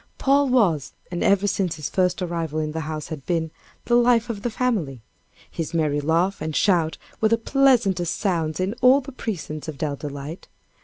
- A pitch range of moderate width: No, wide, 6.1 semitones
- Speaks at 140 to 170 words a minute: No, average, 190 wpm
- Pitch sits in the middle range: Yes, medium, 175 Hz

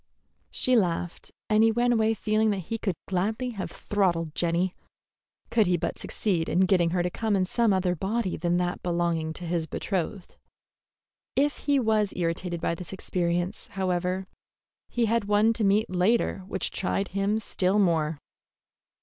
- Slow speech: No, average, 160 wpm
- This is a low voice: No, high, 190 Hz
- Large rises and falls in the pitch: No, average, 3.7 semitones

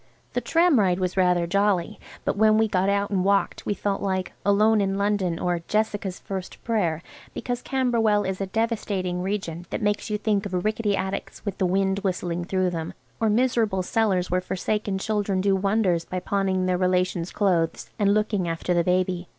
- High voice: Yes, high, 195 Hz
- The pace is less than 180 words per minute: No, average, 185 wpm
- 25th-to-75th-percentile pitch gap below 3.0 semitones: Yes, narrow, 2.4 semitones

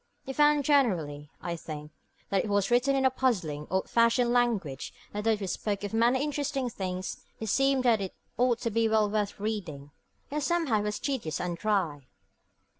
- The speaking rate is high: No, average, 190 wpm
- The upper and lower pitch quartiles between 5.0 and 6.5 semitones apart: Yes, wide, 5.6 semitones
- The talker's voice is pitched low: No, high, 215 Hz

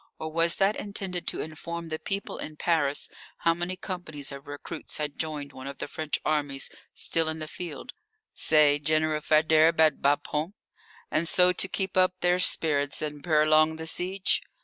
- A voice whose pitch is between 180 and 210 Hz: No, medium, 155 Hz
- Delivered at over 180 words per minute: No, average, 170 wpm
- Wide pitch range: No, average, 2.8 semitones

